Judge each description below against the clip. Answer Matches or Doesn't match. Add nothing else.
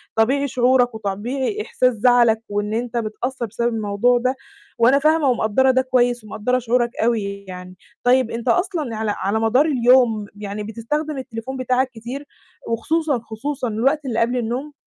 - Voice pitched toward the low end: Doesn't match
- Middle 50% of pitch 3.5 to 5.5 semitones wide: Doesn't match